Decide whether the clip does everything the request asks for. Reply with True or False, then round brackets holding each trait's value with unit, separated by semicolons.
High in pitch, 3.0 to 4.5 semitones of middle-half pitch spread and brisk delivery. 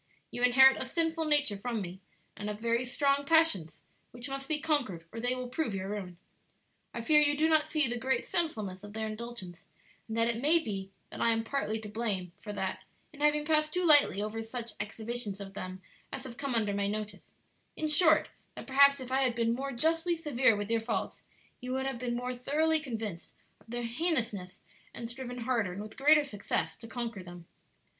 False (240 Hz; 5.1 semitones; 210 wpm)